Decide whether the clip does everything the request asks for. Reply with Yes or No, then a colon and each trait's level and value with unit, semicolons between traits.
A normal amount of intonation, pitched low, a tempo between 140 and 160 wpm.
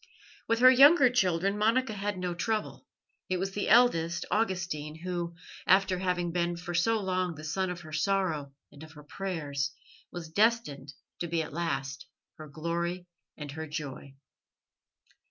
No: average, 3.8 semitones; medium, 175 Hz; average, 155 wpm